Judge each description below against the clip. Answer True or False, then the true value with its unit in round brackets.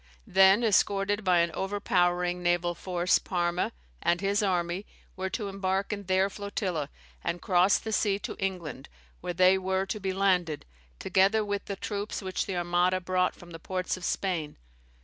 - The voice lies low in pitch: False (185 Hz)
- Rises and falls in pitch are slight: True (1.9 semitones)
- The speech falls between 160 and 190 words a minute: True (170 wpm)